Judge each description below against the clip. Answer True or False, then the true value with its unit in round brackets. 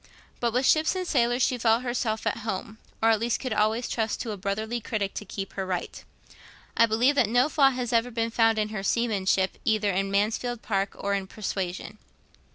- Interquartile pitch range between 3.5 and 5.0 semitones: False (3.1 semitones)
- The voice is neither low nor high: False (220 Hz)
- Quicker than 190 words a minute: True (205 wpm)